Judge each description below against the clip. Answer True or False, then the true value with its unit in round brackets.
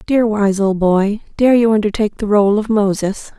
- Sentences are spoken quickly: False (195 wpm)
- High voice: True (210 Hz)